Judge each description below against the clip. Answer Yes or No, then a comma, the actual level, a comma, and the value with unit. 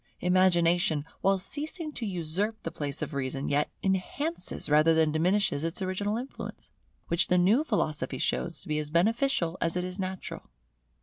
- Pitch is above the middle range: No, medium, 180 Hz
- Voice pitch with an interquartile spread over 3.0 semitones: Yes, average, 4.7 semitones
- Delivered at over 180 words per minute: No, average, 165 wpm